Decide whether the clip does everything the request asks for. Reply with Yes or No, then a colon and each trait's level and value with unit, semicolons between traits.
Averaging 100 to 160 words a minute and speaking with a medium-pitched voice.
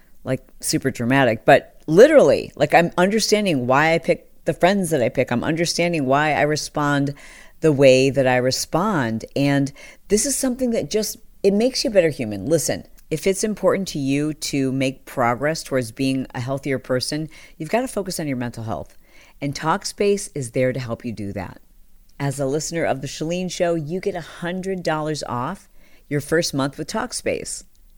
No: average, 180 wpm; medium, 150 Hz